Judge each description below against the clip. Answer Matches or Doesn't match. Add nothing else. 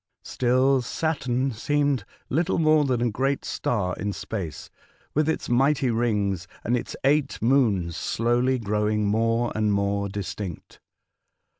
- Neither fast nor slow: Doesn't match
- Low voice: Matches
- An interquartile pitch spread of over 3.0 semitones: Matches